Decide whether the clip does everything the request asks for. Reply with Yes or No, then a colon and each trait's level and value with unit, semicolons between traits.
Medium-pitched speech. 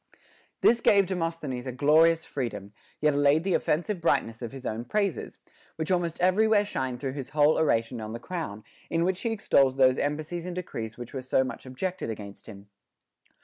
Yes: medium, 145 Hz